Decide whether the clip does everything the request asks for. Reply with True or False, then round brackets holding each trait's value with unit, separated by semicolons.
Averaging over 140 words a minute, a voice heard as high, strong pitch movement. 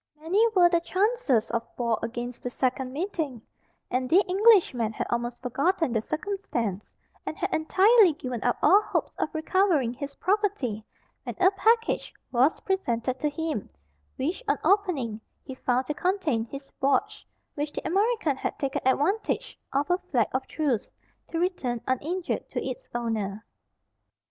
True (155 wpm; 290 Hz; 7.4 semitones)